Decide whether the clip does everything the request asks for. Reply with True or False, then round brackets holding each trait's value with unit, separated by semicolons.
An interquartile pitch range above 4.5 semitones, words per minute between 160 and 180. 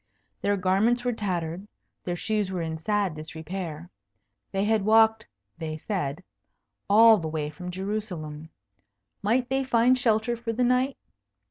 False (5.2 semitones; 140 wpm)